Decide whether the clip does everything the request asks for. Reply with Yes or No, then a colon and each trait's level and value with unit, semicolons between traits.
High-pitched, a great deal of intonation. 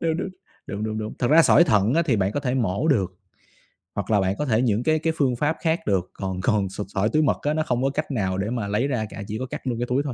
No: low, 120 Hz; wide, 6.3 semitones